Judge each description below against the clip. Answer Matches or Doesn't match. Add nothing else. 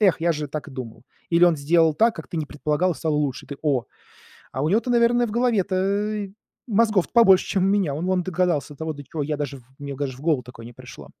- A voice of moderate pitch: Matches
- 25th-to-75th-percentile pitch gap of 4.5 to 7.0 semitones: Matches